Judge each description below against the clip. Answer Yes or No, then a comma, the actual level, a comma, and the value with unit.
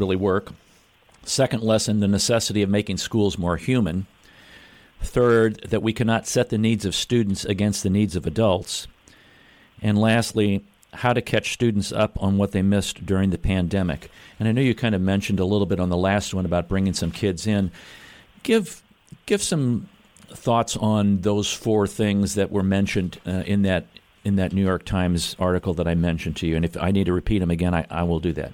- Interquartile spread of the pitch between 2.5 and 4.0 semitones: Yes, average, 3.1 semitones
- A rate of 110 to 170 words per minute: No, average, 200 wpm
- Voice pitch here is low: Yes, low, 100 Hz